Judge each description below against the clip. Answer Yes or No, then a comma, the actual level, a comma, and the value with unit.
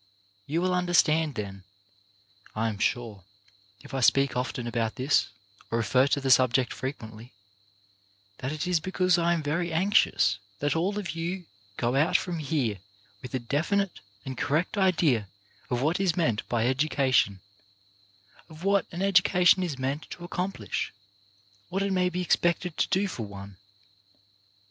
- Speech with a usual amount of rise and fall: No, wide, 6.4 semitones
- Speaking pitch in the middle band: Yes, medium, 150 Hz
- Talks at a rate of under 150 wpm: No, average, 155 wpm